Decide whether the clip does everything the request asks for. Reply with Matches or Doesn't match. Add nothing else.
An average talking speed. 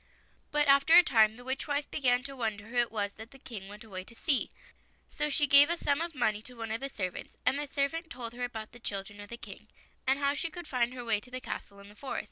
Doesn't match